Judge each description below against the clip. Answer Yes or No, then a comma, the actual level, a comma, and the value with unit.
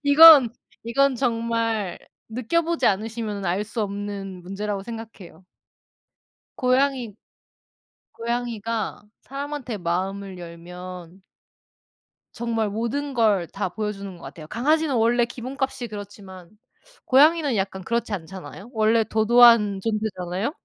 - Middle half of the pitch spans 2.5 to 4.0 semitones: Yes, average, 3.7 semitones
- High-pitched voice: Yes, high, 220 Hz